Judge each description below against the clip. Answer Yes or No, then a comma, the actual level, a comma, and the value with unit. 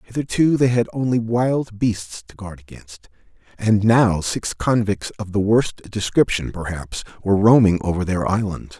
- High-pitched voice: No, low, 105 Hz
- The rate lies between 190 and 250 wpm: No, average, 155 wpm